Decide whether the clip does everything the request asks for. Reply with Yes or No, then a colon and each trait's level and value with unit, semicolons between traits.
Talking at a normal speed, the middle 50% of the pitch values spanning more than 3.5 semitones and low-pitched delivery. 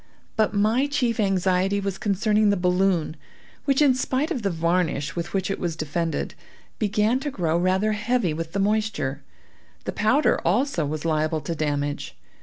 No: average, 165 wpm; average, 4.6 semitones; high, 195 Hz